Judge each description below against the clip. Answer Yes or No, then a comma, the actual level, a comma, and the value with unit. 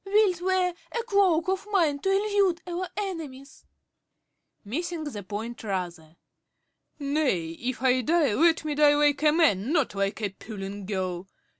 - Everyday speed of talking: Yes, average, 155 wpm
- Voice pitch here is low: No, very high, 295 Hz